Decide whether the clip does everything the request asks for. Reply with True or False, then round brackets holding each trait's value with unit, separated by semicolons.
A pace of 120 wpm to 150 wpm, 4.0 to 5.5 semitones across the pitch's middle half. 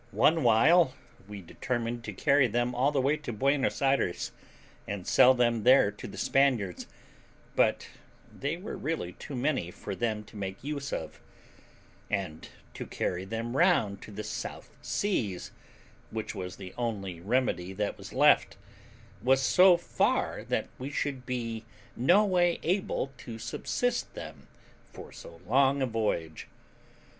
True (145 wpm; 5.2 semitones)